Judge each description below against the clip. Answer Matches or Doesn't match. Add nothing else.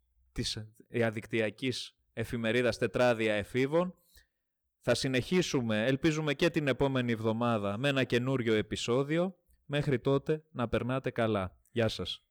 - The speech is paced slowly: Matches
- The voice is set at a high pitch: Doesn't match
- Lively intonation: Doesn't match